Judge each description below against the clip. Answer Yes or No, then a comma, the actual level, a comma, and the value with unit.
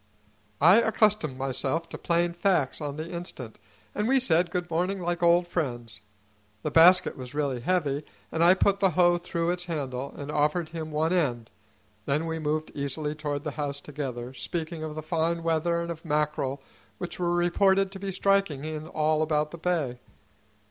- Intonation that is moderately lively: Yes, average, 3.1 semitones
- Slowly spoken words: No, average, 180 wpm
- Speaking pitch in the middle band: Yes, medium, 160 Hz